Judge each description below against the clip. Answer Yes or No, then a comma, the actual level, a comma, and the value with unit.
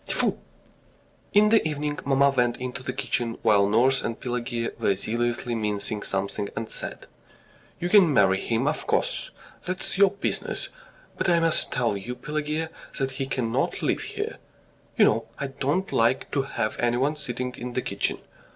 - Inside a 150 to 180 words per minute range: Yes, average, 165 wpm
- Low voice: Yes, low, 125 Hz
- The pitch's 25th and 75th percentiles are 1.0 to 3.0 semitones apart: No, average, 4.6 semitones